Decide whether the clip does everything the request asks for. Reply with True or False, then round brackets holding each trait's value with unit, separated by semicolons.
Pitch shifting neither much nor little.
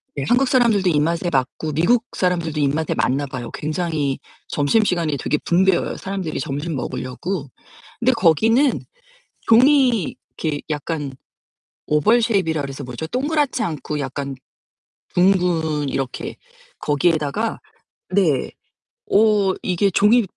False (6.1 semitones)